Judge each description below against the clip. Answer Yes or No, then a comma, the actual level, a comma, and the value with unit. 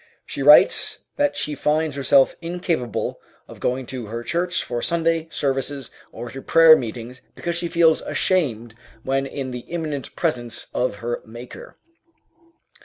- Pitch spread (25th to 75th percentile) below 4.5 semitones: No, average, 5.2 semitones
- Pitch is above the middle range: No, low, 135 Hz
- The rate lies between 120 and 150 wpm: Yes, average, 145 wpm